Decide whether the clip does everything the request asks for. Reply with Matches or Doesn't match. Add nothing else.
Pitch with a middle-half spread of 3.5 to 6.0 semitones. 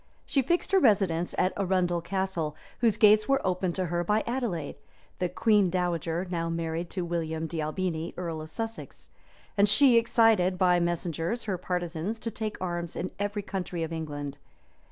Matches